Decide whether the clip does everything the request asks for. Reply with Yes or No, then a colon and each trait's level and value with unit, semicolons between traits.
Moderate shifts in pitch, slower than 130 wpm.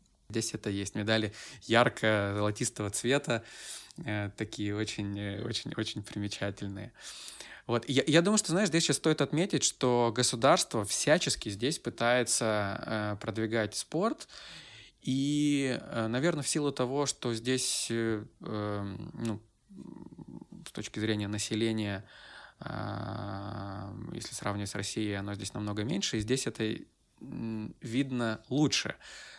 Yes: average, 3.6 semitones; average, 115 wpm